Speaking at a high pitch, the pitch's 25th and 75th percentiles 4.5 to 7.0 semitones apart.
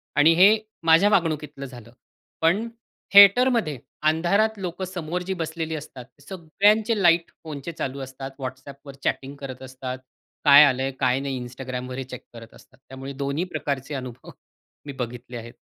No: medium, 145 Hz; average, 4.8 semitones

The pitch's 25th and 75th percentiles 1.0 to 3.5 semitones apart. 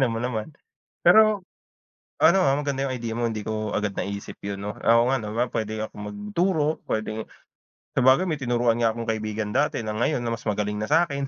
No: average, 4.2 semitones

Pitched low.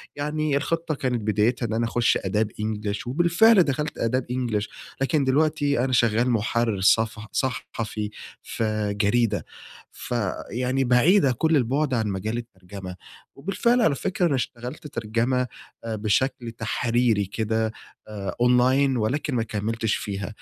Yes: low, 120 Hz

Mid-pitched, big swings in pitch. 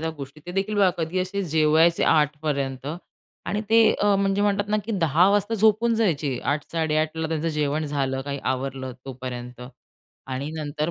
Yes: medium, 155 Hz; wide, 5.7 semitones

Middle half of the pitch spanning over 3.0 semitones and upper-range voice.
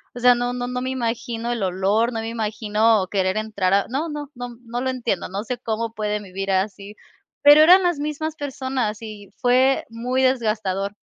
Yes: average, 3.6 semitones; high, 230 Hz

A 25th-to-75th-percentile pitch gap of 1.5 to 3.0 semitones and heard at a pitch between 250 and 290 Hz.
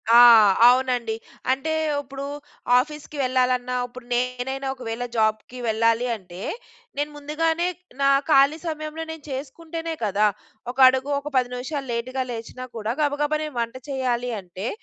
No: average, 3.6 semitones; very high, 255 Hz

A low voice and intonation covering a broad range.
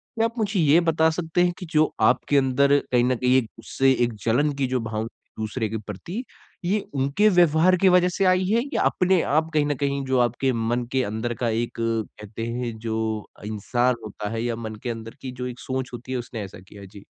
Yes: low, 125 Hz; wide, 5.7 semitones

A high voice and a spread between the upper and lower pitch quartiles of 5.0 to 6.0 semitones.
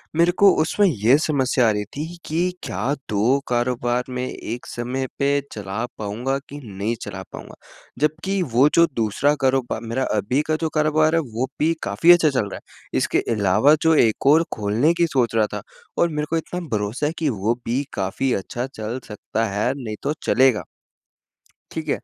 No: low, 130 Hz; wide, 5.6 semitones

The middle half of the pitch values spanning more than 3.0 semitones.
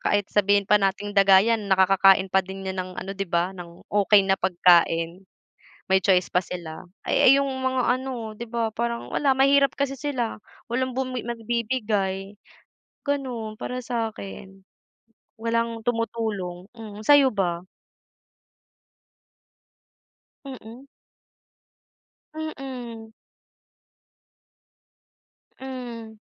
Yes: average, 4.5 semitones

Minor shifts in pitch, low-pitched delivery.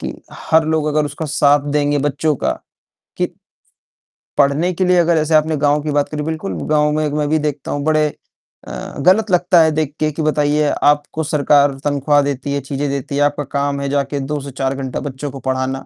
No: narrow, 1.5 semitones; medium, 145 Hz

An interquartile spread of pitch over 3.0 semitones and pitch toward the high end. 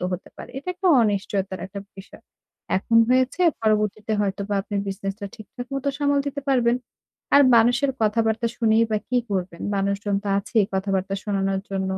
Yes: average, 3.4 semitones; high, 210 Hz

